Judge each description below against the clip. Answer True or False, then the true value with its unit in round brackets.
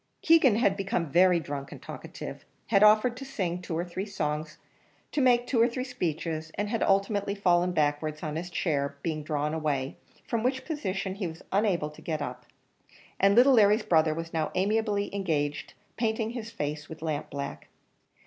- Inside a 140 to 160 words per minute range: False (175 wpm)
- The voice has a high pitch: False (180 Hz)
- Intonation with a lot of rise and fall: True (5.7 semitones)